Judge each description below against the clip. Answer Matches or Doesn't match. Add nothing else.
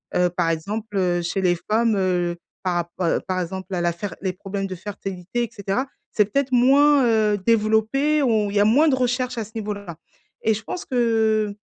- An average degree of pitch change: Matches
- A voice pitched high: Matches